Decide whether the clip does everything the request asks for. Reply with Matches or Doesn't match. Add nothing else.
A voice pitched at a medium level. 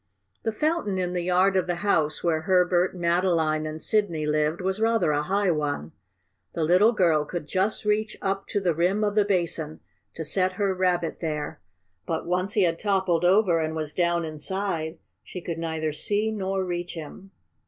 Matches